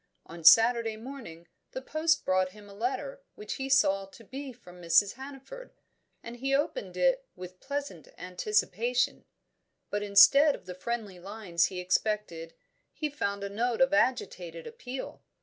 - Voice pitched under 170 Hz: No, high, 225 Hz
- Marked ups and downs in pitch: Yes, wide, 6.5 semitones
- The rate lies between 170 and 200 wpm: No, average, 150 wpm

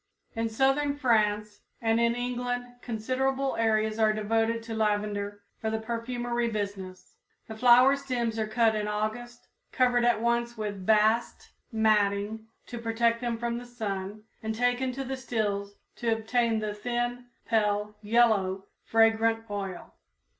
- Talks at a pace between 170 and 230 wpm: No, average, 140 wpm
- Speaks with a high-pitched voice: Yes, high, 225 Hz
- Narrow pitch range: Yes, narrow, 2.2 semitones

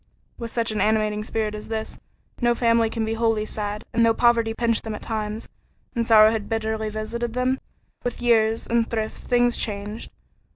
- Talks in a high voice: Yes, high, 225 Hz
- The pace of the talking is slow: No, average, 180 wpm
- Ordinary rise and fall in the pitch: No, narrow, 1.3 semitones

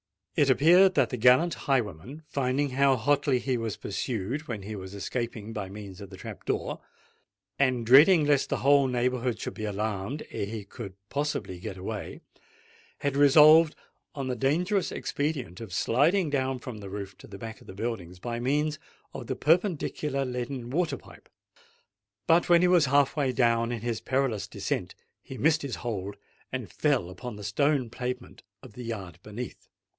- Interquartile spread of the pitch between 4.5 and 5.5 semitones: Yes, average, 5.0 semitones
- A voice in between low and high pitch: No, low, 125 Hz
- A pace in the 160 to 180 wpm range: Yes, average, 175 wpm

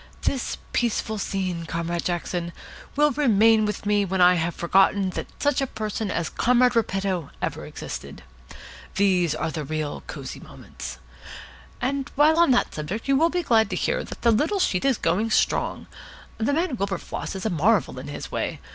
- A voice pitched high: Yes, high, 205 Hz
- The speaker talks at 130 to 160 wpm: No, average, 175 wpm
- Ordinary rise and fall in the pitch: No, wide, 5.9 semitones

